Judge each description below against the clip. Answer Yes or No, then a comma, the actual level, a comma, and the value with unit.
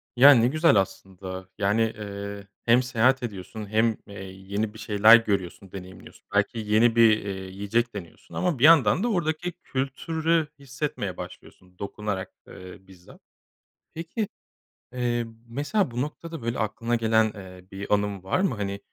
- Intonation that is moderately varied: Yes, average, 4.6 semitones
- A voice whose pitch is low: Yes, low, 110 Hz